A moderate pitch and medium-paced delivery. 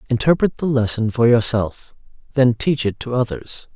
No: low, 120 Hz; average, 160 wpm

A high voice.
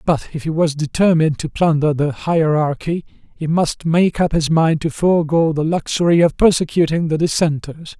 No: medium, 160 Hz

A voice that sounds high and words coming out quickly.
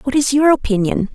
Yes: very high, 255 Hz; fast, 210 wpm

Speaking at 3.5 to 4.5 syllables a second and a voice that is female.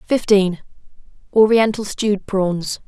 Yes: 4.0 syllables/s; female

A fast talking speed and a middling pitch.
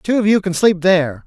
Yes: fast, 285 wpm; medium, 180 Hz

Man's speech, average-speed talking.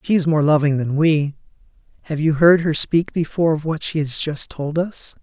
No: male; fast, 220 wpm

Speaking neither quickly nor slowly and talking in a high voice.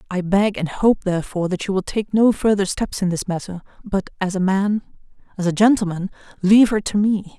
No: fast, 210 wpm; high, 195 Hz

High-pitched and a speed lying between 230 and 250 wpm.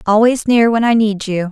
Yes: high, 220 Hz; fast, 240 wpm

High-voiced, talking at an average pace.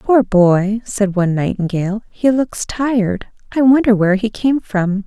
Yes: high, 215 Hz; average, 165 wpm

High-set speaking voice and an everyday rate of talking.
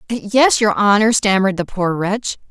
Yes: high, 205 Hz; average, 170 wpm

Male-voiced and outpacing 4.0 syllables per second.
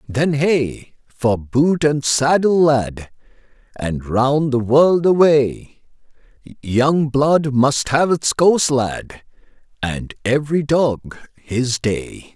No: male; 2.9 syllables/s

